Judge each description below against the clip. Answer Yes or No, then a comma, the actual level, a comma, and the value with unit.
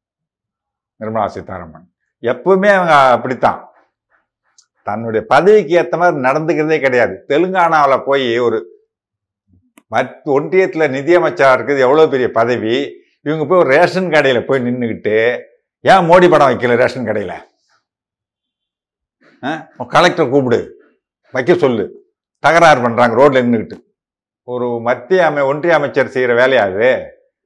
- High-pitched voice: No, medium, 150 Hz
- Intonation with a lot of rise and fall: Yes, wide, 7.4 semitones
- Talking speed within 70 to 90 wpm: No, average, 110 wpm